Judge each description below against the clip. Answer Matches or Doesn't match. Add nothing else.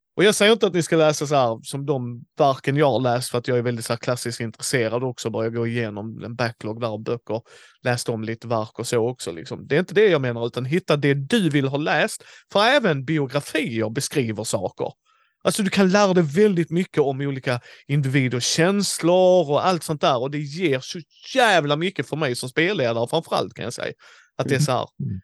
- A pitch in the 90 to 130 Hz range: Doesn't match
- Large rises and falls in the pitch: Matches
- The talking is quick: Matches